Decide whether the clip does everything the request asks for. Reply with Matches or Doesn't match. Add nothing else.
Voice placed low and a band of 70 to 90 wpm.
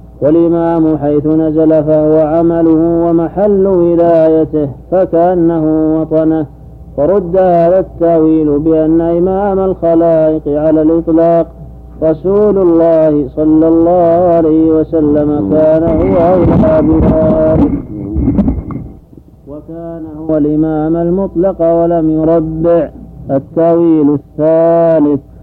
Doesn't match